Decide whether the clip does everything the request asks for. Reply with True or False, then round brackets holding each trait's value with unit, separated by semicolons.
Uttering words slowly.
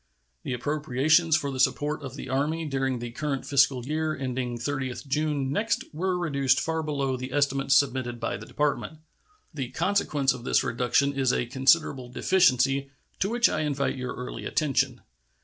False (165 wpm)